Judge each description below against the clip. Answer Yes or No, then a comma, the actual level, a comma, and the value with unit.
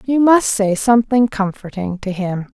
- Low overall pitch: No, high, 210 Hz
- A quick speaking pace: No, average, 165 wpm